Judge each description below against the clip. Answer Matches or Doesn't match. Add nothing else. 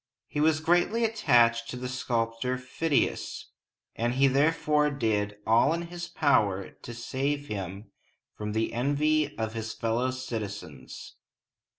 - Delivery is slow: Matches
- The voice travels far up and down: Doesn't match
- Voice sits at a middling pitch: Doesn't match